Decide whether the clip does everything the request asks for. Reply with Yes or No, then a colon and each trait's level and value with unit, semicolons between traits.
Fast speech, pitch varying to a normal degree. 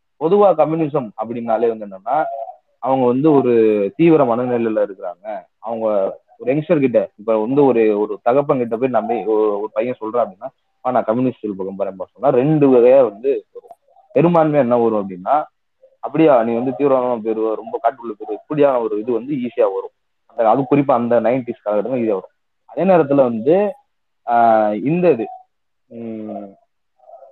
No: fast, 145 wpm; wide, 6.7 semitones